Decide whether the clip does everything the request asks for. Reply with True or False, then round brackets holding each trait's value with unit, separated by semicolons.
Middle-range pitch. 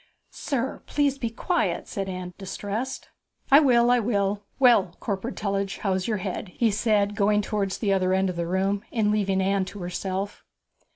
False (200 Hz)